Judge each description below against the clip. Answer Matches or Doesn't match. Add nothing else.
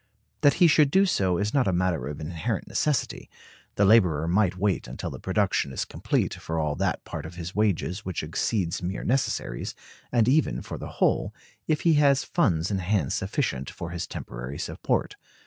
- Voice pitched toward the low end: Matches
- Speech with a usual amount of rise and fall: Doesn't match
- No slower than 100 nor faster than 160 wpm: Doesn't match